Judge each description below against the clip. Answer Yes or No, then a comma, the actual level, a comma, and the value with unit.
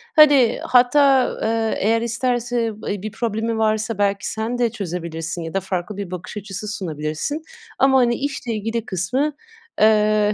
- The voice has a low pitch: No, high, 220 Hz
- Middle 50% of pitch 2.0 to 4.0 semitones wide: Yes, average, 3.5 semitones